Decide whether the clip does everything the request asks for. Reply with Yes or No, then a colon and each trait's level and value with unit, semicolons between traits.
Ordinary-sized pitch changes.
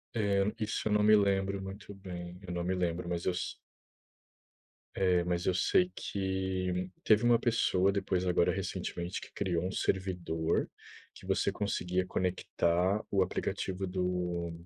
No: narrow, 1.8 semitones